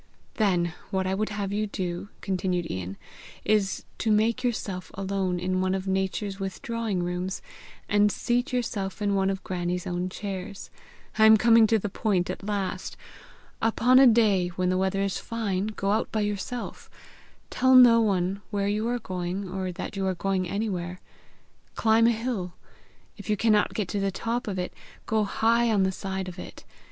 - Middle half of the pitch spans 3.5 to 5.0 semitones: No, average, 2.8 semitones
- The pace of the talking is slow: No, average, 180 wpm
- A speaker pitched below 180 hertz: No, high, 195 Hz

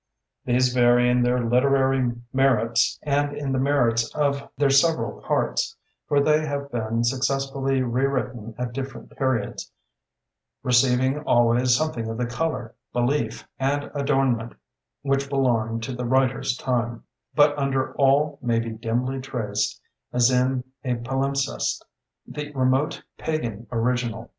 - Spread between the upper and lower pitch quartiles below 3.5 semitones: Yes, narrow, 2.4 semitones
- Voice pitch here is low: Yes, low, 130 Hz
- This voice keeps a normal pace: No, slow, 130 wpm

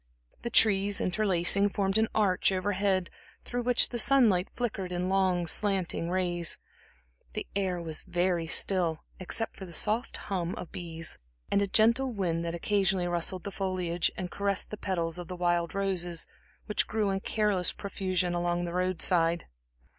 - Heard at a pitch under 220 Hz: Yes, medium, 185 Hz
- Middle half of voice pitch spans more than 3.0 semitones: No, narrow, 2.6 semitones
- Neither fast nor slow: Yes, average, 165 wpm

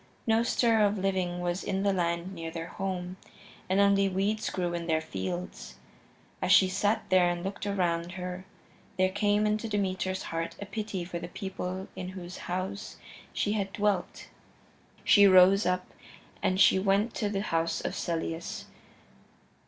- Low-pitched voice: No, high, 190 Hz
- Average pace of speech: Yes, average, 160 wpm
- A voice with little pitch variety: Yes, narrow, 2.3 semitones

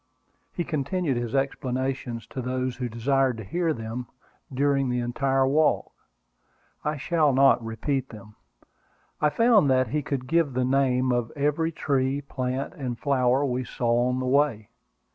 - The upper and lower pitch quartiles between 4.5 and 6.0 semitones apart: No, narrow, 2.5 semitones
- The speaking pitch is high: No, low, 130 Hz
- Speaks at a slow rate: No, average, 155 wpm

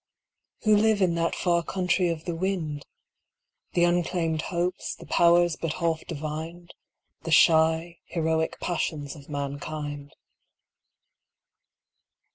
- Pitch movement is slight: Yes, narrow, 1.9 semitones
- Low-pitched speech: No, medium, 165 Hz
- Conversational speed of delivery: No, slow, 100 wpm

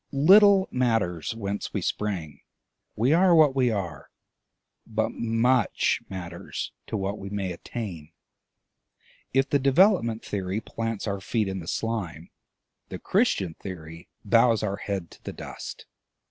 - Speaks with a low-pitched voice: Yes, low, 105 Hz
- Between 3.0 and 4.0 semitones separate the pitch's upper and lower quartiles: No, average, 5.0 semitones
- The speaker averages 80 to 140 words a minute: Yes, slow, 135 wpm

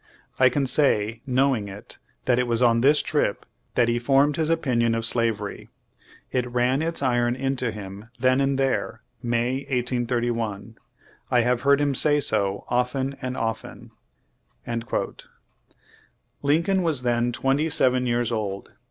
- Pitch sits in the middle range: No, low, 125 Hz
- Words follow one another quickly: No, average, 145 wpm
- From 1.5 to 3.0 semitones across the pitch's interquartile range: Yes, average, 2.7 semitones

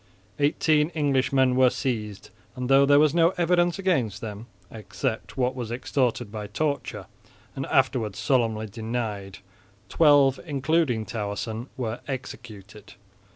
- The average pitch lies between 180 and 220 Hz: No, low, 125 Hz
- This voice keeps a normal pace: No, slow, 120 wpm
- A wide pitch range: No, average, 4.5 semitones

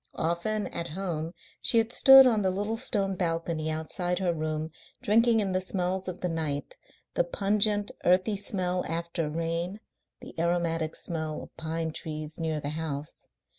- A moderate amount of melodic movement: Yes, average, 3.5 semitones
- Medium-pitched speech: Yes, medium, 170 Hz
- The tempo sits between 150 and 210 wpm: Yes, average, 160 wpm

